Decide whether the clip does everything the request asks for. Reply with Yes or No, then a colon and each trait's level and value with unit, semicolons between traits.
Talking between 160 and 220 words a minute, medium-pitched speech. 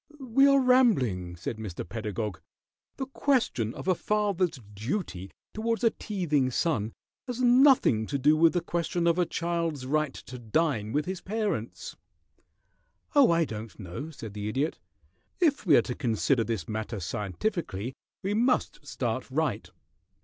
No: average, 150 wpm; medium, 155 Hz